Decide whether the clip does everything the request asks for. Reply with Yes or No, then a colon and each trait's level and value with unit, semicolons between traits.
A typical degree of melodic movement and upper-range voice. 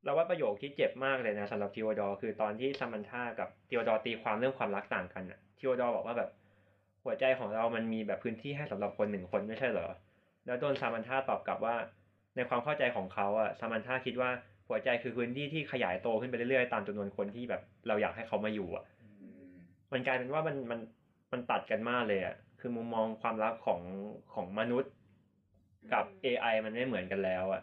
No: average, 3.9 semitones; low, 110 Hz